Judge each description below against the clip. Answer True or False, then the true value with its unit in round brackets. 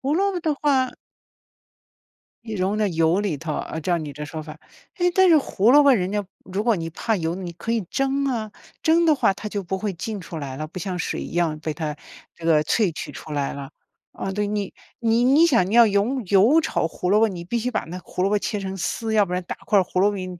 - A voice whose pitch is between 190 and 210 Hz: True (200 Hz)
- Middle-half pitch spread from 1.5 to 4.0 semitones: False (5.6 semitones)